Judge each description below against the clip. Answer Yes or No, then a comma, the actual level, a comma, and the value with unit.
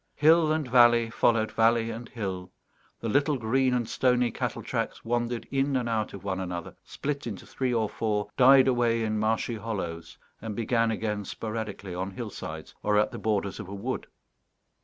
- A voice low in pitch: Yes, low, 115 Hz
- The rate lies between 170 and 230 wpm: Yes, average, 180 wpm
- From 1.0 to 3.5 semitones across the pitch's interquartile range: Yes, average, 2.9 semitones